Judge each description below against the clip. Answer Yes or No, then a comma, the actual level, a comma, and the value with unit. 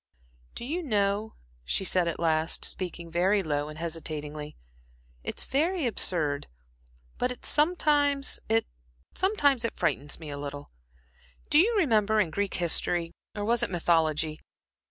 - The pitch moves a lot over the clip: Yes, wide, 8.1 semitones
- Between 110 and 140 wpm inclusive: Yes, slow, 135 wpm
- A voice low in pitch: No, medium, 180 Hz